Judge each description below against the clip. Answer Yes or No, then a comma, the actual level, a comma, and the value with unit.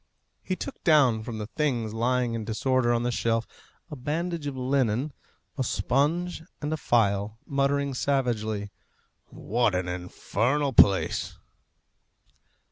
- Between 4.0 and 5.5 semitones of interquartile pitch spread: Yes, average, 4.3 semitones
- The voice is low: Yes, low, 125 Hz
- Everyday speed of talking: No, slow, 125 wpm